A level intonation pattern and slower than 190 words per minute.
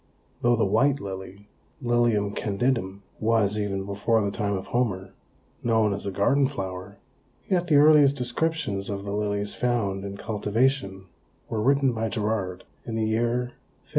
No: average, 3.5 semitones; average, 155 wpm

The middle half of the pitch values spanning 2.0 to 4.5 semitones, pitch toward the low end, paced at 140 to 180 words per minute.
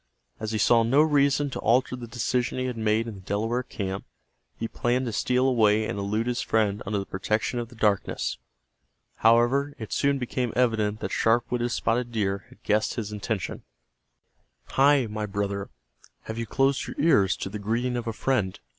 No: average, 3.0 semitones; low, 115 Hz; average, 190 wpm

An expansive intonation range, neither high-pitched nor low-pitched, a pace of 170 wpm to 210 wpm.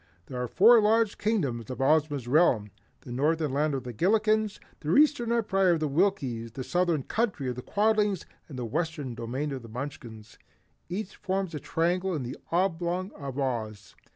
Yes: wide, 7.2 semitones; medium, 155 Hz; average, 180 wpm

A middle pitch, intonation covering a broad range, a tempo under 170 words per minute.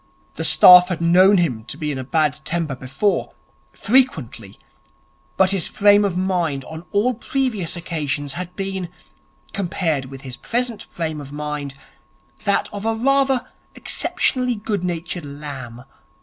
Yes: medium, 175 Hz; wide, 5.7 semitones; average, 145 wpm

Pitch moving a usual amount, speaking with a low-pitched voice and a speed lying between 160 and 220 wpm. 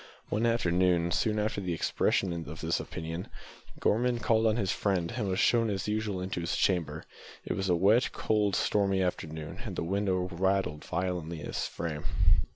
Yes: average, 3.7 semitones; very low, 95 Hz; average, 175 wpm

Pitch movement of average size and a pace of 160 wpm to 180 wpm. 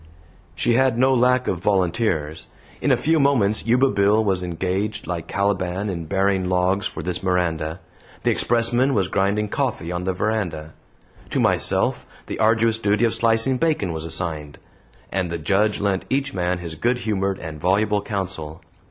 Yes: average, 4.1 semitones; average, 165 wpm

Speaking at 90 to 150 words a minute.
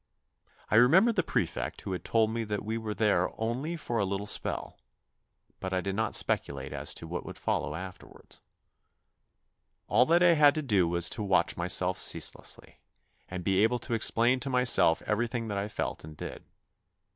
No: average, 180 wpm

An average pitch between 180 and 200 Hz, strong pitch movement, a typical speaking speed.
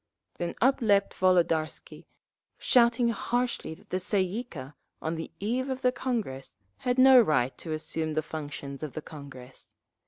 Yes: medium, 185 Hz; wide, 7.6 semitones; average, 160 wpm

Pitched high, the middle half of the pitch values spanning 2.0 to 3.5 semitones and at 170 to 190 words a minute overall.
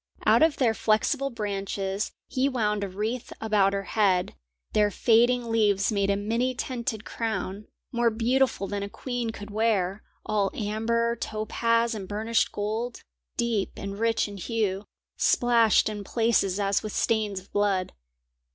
No: high, 215 Hz; narrow, 2.5 semitones; average, 150 wpm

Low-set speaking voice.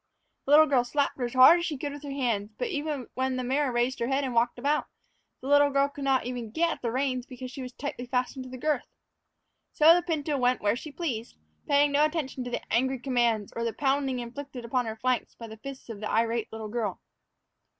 No: very high, 260 Hz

